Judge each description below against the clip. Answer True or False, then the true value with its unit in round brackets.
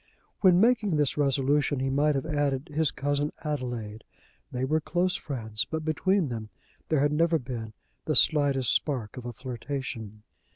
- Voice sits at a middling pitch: True (145 Hz)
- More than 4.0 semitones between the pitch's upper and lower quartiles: False (3.7 semitones)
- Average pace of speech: True (160 wpm)